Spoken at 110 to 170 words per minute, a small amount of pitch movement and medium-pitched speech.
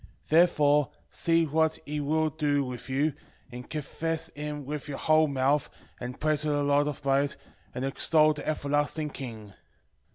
Yes: average, 155 wpm; narrow, 1.9 semitones; medium, 145 Hz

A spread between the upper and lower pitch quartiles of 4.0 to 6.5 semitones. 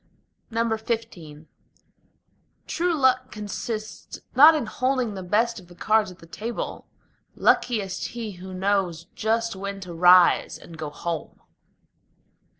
Yes: average, 4.4 semitones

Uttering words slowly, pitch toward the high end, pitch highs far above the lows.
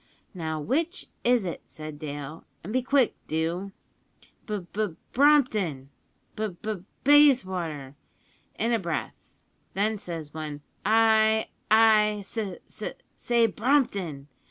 Yes: slow, 125 wpm; high, 205 Hz; wide, 6.0 semitones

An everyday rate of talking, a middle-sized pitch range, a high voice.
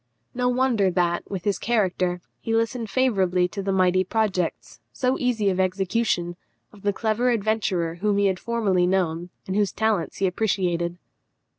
Yes: average, 160 wpm; average, 3.6 semitones; high, 195 Hz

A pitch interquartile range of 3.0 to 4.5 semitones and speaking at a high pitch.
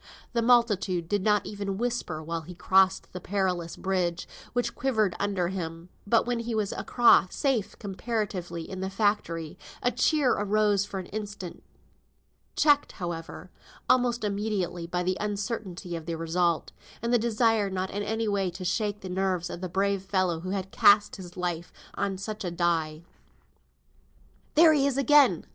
Yes: average, 3.4 semitones; high, 195 Hz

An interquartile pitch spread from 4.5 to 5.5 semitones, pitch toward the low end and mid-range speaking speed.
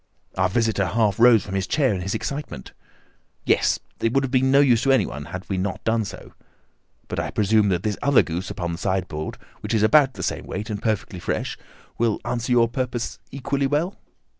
No: average, 5.2 semitones; low, 110 Hz; fast, 210 wpm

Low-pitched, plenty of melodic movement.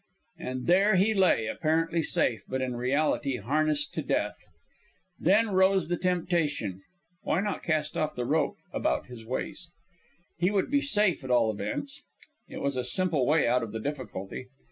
No: medium, 155 Hz; wide, 6.3 semitones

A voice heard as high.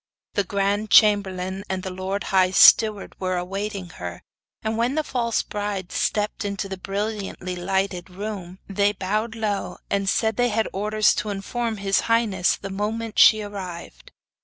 Yes: high, 200 Hz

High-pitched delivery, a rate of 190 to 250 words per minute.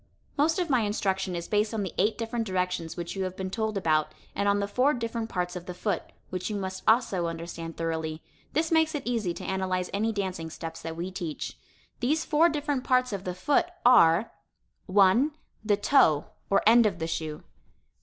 Yes: high, 195 Hz; average, 200 wpm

